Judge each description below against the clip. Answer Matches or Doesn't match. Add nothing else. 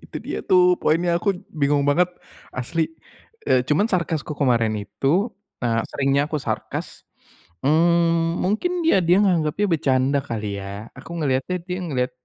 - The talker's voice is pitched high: Doesn't match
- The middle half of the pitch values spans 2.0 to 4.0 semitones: Doesn't match